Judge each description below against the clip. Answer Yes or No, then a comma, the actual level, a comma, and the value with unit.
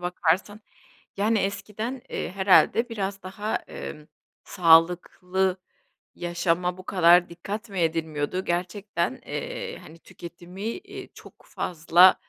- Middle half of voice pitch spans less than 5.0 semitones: Yes, average, 3.0 semitones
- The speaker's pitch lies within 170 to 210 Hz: Yes, medium, 185 Hz